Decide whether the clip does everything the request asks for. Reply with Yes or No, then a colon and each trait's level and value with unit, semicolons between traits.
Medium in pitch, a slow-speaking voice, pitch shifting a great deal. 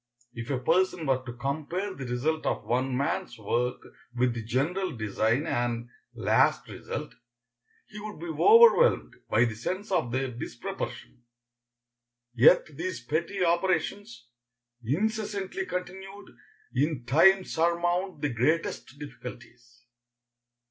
Yes: medium, 150 Hz; slow, 120 wpm; wide, 7.2 semitones